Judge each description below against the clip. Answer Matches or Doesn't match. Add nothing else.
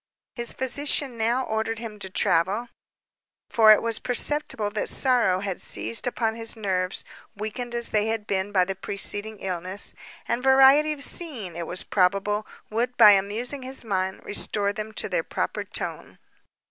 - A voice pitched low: Doesn't match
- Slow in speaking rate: Doesn't match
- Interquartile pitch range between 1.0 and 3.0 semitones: Doesn't match